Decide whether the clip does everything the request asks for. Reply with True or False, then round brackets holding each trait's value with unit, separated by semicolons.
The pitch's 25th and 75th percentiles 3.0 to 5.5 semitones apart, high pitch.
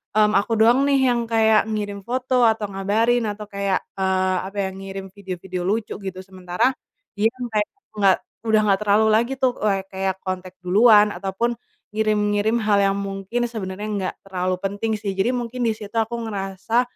False (2.6 semitones; 205 Hz)